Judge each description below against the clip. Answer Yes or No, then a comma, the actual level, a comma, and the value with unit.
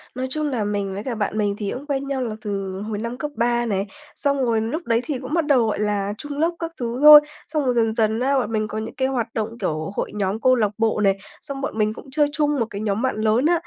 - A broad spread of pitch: No, average, 4.5 semitones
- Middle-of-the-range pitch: No, high, 230 Hz